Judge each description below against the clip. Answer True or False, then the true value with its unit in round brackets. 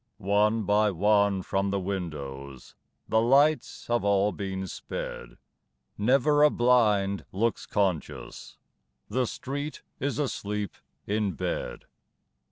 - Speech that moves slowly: True (110 wpm)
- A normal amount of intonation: True (3.7 semitones)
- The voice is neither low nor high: False (105 Hz)